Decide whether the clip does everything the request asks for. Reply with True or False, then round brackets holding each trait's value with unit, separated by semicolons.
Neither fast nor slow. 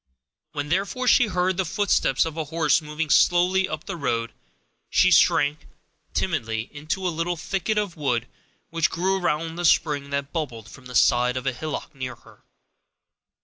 True (170 wpm)